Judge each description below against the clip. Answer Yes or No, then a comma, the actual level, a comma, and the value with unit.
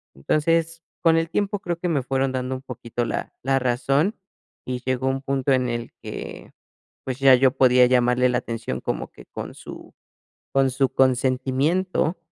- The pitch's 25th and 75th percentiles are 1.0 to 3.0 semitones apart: No, average, 3.4 semitones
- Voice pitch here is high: No, low, 130 Hz